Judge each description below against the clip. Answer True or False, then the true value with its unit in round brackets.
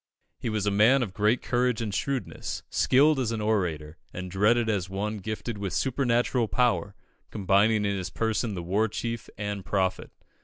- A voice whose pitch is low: True (105 Hz)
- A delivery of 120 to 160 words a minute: False (175 wpm)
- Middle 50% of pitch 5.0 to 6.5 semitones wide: False (3.2 semitones)